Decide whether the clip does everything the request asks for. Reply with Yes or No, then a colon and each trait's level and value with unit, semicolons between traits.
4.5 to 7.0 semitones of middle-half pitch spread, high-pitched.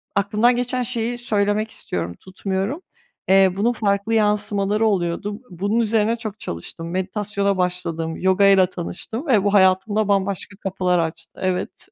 No: narrow, 2.6 semitones; high, 200 Hz